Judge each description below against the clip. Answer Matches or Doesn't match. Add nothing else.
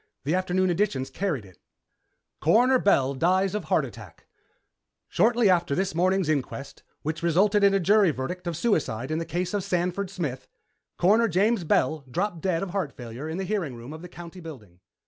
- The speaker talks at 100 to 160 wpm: Doesn't match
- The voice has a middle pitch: Matches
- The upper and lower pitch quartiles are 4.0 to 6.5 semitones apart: Matches